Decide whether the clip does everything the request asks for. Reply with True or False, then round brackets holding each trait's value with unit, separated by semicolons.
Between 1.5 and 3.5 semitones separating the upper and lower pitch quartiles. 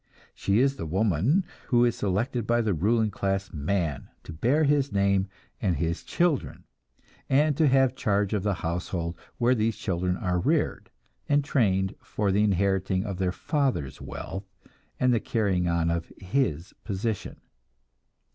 False (5.0 semitones)